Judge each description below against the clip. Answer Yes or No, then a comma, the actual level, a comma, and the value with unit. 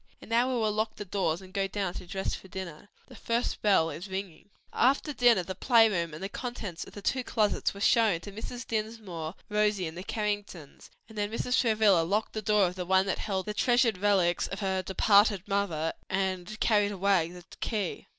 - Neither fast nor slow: No, fast, 210 wpm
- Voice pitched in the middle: No, high, 200 Hz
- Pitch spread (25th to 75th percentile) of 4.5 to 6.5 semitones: No, average, 2.7 semitones